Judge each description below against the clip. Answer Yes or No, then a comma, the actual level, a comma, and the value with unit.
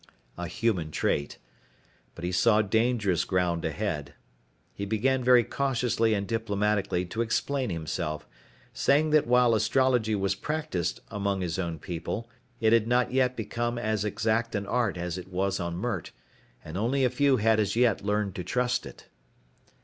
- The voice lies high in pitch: No, low, 110 Hz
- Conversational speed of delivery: Yes, average, 160 wpm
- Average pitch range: Yes, average, 4.6 semitones